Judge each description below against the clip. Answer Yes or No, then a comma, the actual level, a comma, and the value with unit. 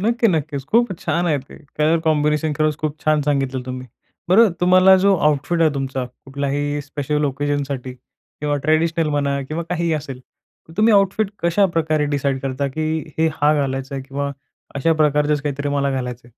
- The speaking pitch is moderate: Yes, medium, 150 Hz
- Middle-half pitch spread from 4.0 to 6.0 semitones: No, average, 2.8 semitones